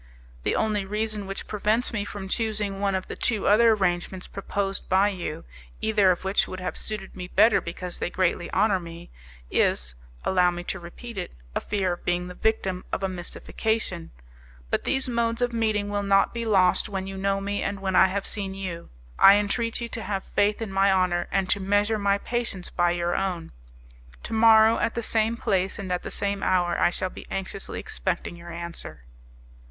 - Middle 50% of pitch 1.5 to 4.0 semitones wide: Yes, average, 2.7 semitones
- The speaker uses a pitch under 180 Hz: No, high, 195 Hz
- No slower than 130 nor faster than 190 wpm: No, average, 200 wpm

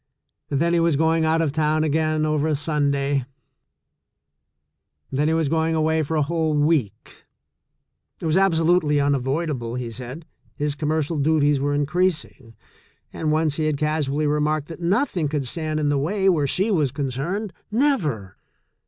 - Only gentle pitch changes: Yes, narrow, 2.2 semitones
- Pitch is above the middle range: No, medium, 155 Hz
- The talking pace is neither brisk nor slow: Yes, average, 170 wpm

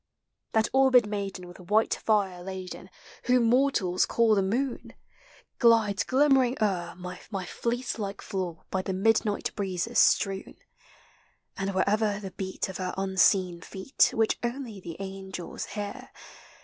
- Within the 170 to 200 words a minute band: No, average, 140 wpm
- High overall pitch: Yes, high, 200 Hz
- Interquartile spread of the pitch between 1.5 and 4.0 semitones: Yes, average, 3.5 semitones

